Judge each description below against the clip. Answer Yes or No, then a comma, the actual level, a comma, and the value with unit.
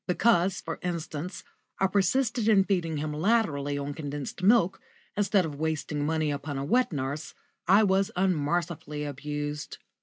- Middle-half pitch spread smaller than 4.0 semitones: No, average, 4.7 semitones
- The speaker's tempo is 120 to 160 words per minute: Yes, average, 145 wpm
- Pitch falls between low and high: Yes, medium, 160 Hz